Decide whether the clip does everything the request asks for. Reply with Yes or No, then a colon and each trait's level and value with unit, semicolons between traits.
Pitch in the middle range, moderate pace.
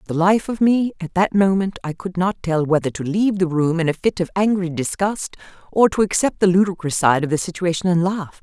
No: medium, 180 Hz; fast, 240 wpm